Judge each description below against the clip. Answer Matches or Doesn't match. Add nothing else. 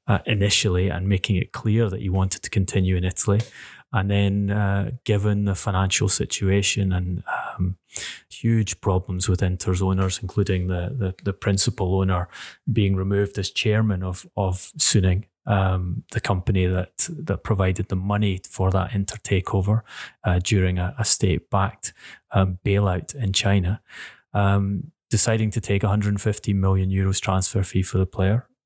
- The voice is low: Matches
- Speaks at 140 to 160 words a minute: Matches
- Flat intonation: Matches